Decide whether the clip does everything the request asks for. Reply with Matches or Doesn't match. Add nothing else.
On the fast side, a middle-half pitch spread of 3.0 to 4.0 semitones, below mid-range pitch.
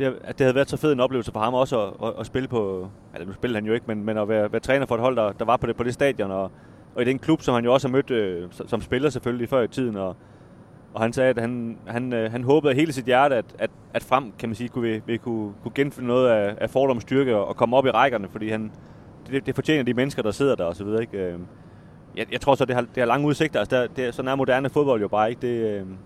Matches